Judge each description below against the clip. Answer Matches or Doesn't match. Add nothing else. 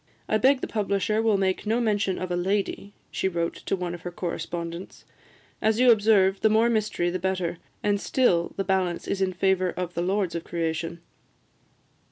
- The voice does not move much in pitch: Doesn't match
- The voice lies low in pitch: Doesn't match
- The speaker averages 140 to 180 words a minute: Doesn't match